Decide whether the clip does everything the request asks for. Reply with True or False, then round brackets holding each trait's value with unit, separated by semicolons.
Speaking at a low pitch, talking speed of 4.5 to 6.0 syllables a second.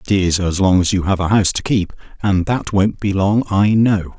True (95 Hz; 5.1 syllables/s)